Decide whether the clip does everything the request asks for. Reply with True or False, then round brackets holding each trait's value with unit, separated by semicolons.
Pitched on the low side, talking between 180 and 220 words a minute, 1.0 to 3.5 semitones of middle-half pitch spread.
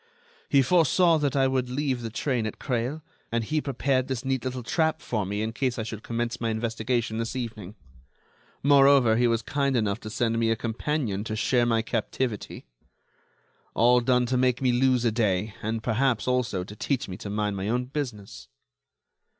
True (120 Hz; 190 wpm; 3.0 semitones)